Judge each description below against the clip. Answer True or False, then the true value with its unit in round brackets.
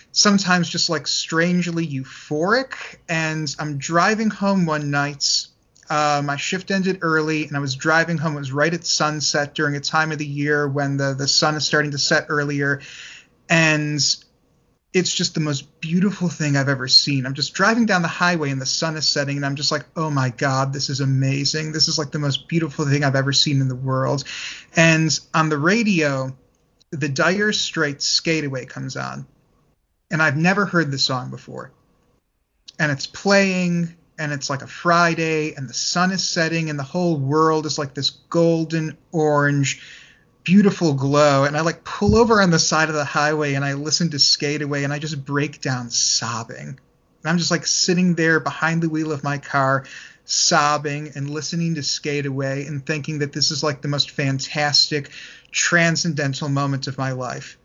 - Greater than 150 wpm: True (190 wpm)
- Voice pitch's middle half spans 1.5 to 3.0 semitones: True (2.6 semitones)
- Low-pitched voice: False (150 Hz)